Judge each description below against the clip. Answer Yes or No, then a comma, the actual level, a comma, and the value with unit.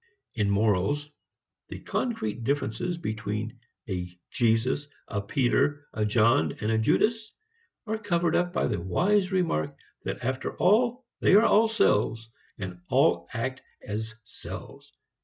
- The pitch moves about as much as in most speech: No, wide, 8.9 semitones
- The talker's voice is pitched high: No, low, 120 Hz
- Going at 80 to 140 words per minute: Yes, slow, 135 wpm